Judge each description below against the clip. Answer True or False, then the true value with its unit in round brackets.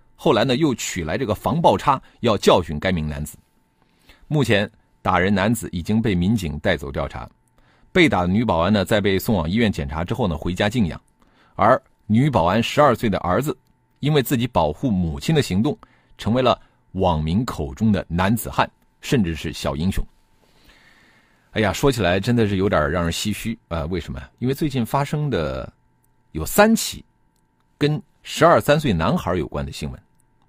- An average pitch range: False (6.4 semitones)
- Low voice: True (100 Hz)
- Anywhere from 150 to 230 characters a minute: False (265 characters per minute)